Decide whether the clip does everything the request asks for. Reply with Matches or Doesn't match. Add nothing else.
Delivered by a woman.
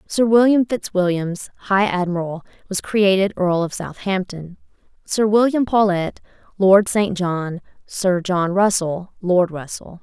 Matches